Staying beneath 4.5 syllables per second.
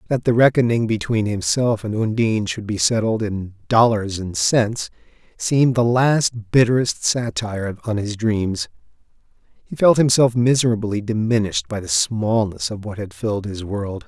No: 4.8 syllables/s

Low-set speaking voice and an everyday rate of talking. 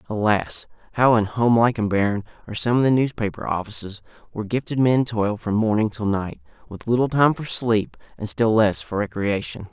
Yes: low, 110 Hz; average, 180 wpm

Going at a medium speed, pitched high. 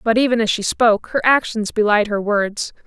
No: fast, 210 wpm; high, 220 Hz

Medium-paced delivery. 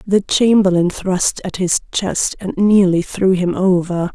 Yes: average, 160 wpm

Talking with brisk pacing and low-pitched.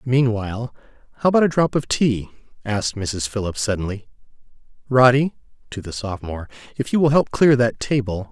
No: average, 145 wpm; low, 115 Hz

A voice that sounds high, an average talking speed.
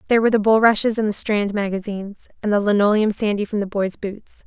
No: high, 210 Hz; fast, 215 wpm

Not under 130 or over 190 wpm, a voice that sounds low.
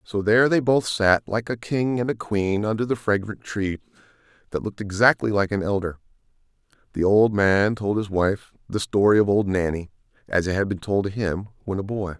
No: average, 200 wpm; low, 105 Hz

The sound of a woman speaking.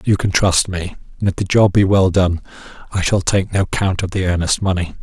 No: male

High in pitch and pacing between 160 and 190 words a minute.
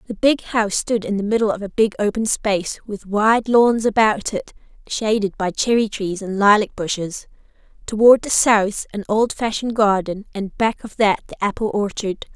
Yes: high, 210 Hz; average, 180 wpm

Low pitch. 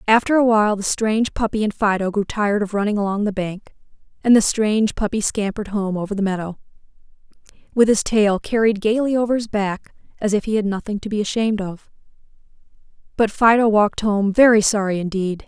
No: high, 210 Hz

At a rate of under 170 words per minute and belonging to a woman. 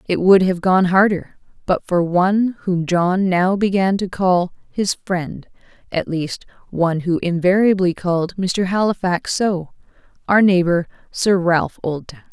Yes: average, 140 wpm; female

